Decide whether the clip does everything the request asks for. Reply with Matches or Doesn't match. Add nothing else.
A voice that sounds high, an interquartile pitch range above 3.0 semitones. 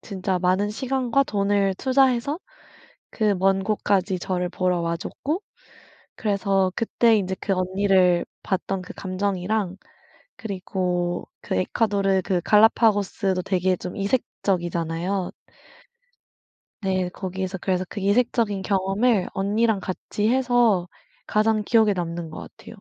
Doesn't match